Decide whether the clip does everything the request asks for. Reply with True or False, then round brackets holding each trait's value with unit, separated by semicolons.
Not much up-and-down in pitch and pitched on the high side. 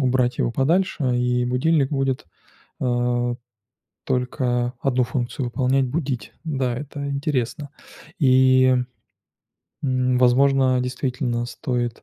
False (1.8 semitones; 130 Hz)